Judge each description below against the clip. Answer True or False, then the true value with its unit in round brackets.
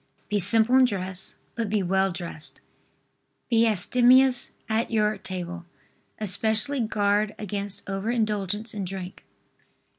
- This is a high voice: True (210 Hz)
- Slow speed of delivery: True (120 wpm)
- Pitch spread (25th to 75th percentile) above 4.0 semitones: False (2.9 semitones)